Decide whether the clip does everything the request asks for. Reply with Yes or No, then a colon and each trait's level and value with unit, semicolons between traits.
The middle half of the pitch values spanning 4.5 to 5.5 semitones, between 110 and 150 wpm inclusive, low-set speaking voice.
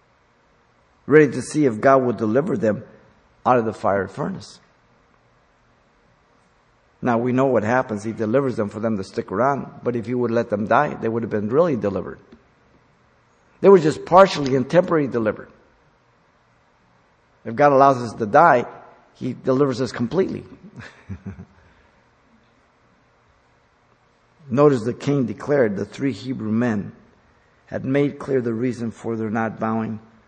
No: average, 3.8 semitones; average, 145 wpm; low, 120 Hz